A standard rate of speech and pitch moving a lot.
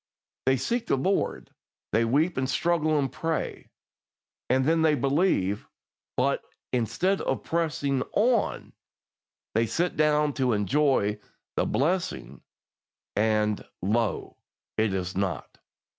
No: slow, 115 wpm; wide, 6.5 semitones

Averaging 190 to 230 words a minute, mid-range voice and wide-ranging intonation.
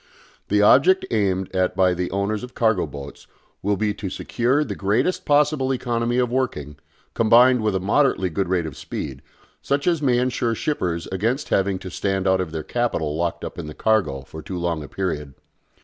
No: average, 195 wpm; low, 100 Hz; wide, 5.7 semitones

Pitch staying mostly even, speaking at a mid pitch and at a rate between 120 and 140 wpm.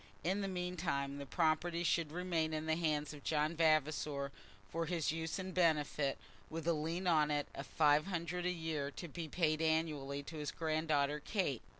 No: narrow, 2.3 semitones; medium, 160 Hz; average, 185 wpm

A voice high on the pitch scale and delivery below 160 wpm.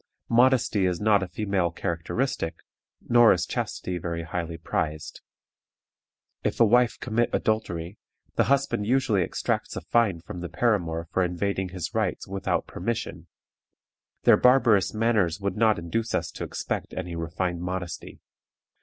No: very low, 95 Hz; average, 140 wpm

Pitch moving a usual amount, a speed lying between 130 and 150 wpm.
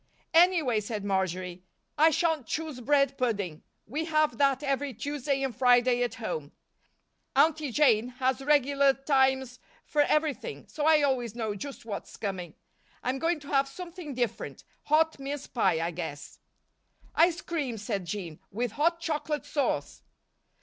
Yes: average, 4.9 semitones; average, 145 wpm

